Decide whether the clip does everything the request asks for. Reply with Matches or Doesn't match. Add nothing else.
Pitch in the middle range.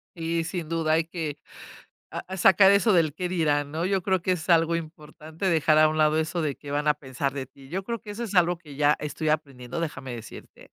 Matches